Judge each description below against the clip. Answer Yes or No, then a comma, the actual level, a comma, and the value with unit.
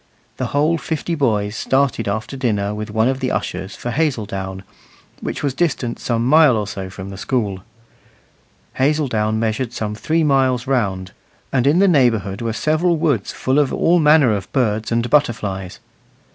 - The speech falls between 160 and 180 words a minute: Yes, average, 165 wpm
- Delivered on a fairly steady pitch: No, average, 5.3 semitones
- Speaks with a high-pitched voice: No, low, 120 Hz